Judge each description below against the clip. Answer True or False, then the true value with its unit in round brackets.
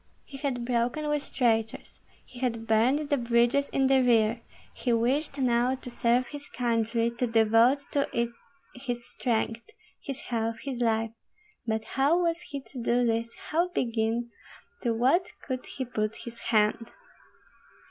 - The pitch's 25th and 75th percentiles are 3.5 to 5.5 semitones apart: False (2.8 semitones)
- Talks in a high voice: True (240 Hz)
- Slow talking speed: False (155 wpm)